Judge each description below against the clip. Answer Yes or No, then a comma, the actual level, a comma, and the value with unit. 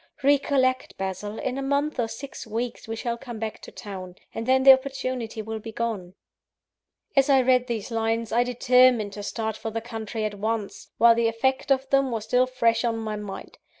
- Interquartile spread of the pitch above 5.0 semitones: No, average, 2.7 semitones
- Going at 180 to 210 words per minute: Yes, average, 200 wpm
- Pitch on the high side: Yes, high, 230 Hz